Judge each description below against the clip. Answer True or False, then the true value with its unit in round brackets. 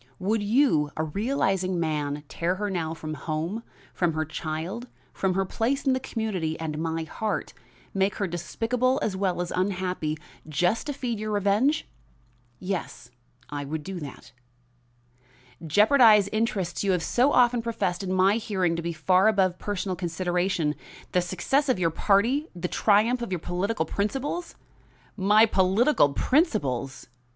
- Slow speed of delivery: False (150 wpm)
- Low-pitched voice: False (190 Hz)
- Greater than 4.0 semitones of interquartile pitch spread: True (4.8 semitones)